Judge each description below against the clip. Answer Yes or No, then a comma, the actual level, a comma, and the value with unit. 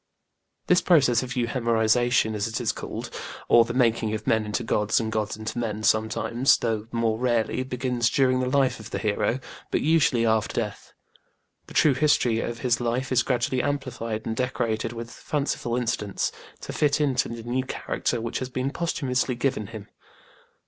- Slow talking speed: No, average, 175 wpm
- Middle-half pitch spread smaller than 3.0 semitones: Yes, narrow, 2.5 semitones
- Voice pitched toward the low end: Yes, low, 120 Hz